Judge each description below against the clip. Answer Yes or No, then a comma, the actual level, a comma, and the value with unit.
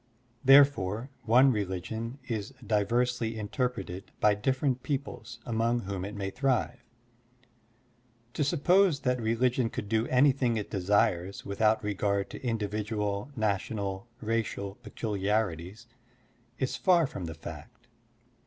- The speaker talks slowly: Yes, slow, 115 wpm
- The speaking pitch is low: Yes, low, 110 Hz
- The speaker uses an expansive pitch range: No, average, 3.9 semitones